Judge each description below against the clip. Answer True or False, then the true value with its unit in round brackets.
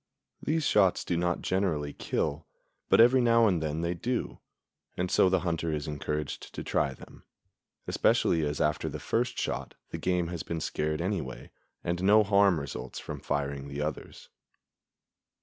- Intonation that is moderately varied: True (4.1 semitones)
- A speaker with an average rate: True (165 wpm)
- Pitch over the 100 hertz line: False (85 Hz)